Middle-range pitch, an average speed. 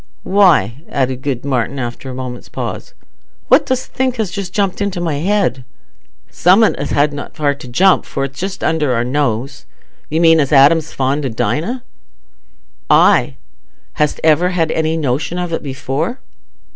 Yes: medium, 150 Hz; average, 160 wpm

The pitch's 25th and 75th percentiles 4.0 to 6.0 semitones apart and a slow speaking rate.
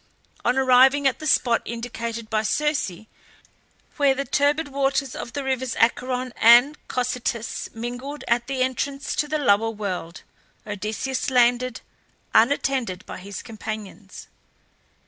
No: average, 3.3 semitones; slow, 125 wpm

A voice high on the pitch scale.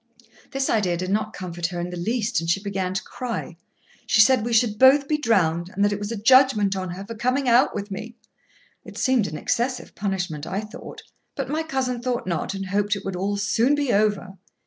Yes: high, 210 Hz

